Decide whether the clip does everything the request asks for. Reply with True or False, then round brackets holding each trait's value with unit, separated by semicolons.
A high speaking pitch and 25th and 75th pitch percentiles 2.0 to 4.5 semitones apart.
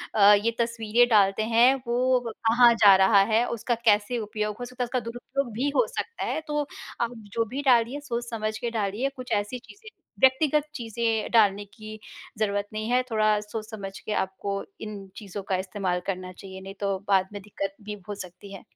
True (215 Hz; 3.0 semitones)